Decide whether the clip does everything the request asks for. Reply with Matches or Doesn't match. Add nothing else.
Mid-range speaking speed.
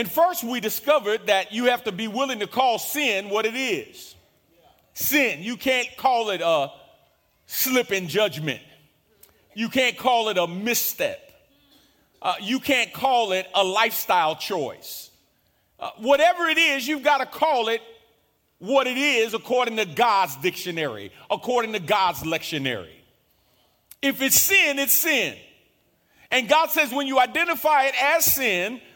Matches